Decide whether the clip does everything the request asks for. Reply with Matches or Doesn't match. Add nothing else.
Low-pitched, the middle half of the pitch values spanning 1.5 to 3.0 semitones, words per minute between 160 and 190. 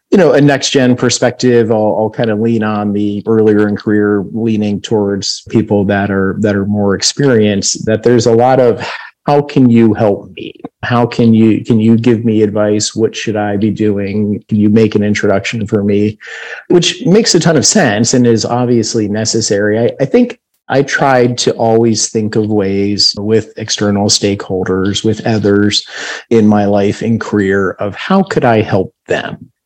Matches